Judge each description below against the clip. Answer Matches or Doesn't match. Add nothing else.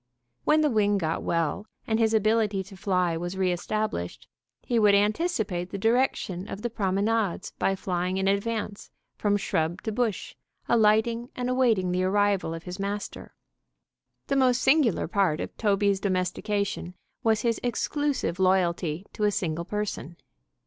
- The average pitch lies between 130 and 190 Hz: Doesn't match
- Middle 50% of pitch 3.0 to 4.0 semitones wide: Matches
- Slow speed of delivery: Doesn't match